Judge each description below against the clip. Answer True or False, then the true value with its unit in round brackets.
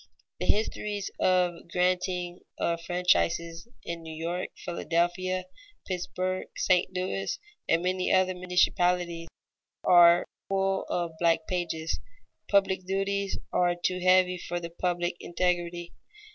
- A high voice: False (180 Hz)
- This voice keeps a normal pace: False (115 wpm)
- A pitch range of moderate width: False (1.3 semitones)